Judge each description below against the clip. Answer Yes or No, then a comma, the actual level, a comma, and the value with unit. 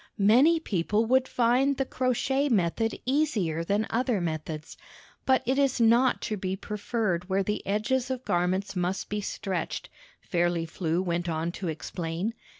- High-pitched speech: Yes, high, 205 Hz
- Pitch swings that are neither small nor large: No, wide, 6.3 semitones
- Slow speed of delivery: No, average, 155 wpm